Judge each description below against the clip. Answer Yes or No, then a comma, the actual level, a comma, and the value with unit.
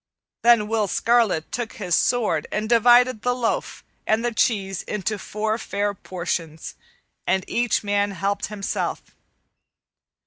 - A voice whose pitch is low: No, high, 210 Hz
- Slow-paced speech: Yes, slow, 130 wpm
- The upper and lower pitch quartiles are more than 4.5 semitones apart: No, average, 3.1 semitones